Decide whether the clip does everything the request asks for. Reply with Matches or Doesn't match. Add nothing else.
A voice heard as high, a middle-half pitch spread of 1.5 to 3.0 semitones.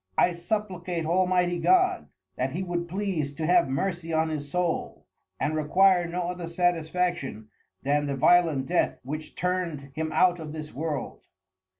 Doesn't match